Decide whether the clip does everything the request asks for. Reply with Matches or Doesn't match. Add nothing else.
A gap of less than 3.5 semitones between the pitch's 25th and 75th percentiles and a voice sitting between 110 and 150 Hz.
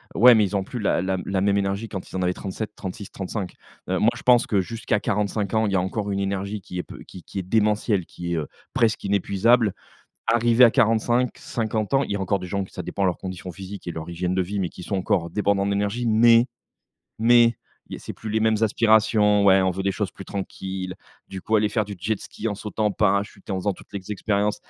Doesn't match